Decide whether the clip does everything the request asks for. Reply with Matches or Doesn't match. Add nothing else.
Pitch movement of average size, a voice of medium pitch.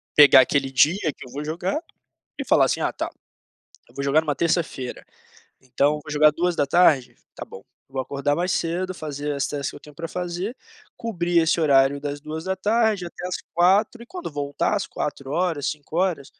Matches